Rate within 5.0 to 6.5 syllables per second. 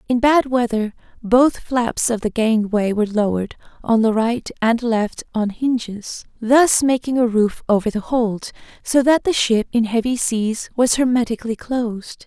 No: 4.5 syllables/s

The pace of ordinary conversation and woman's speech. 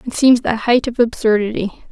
Yes: average, 190 wpm; female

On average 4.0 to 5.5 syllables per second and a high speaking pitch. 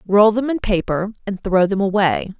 Yes: 4.9 syllables/s; high, 200 Hz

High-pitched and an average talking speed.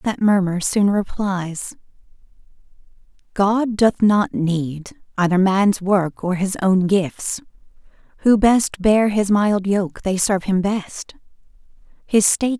No: high, 200 Hz; slow, 130 wpm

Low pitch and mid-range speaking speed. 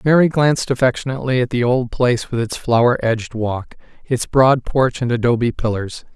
Yes: low, 125 Hz; average, 175 wpm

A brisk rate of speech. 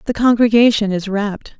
No: average, 150 wpm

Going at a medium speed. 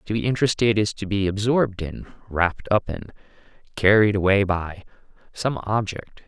Yes: average, 155 wpm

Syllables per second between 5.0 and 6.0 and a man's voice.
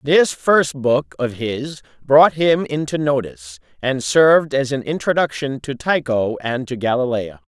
No: 4.2 syllables/s; male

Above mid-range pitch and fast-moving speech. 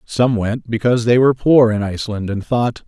No: low, 115 Hz; fast, 210 wpm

